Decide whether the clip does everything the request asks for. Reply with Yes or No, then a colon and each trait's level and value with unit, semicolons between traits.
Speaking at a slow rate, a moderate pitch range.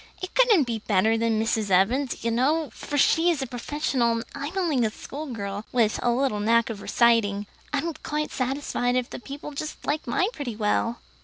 No: average, 190 wpm; average, 4.6 semitones